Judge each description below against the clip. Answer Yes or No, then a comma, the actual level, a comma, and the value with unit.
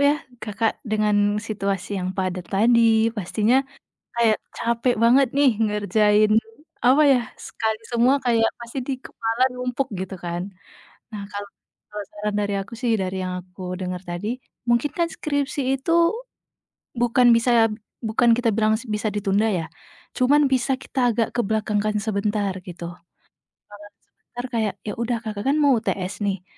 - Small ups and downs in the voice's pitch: No, average, 3.2 semitones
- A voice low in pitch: No, high, 220 Hz